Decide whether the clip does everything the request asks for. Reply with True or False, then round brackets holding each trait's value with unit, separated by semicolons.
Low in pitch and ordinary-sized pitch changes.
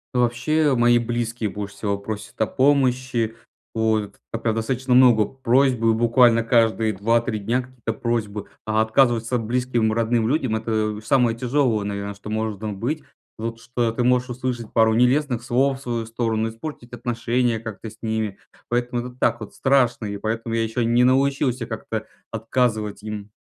False (115 Hz; 2.1 semitones)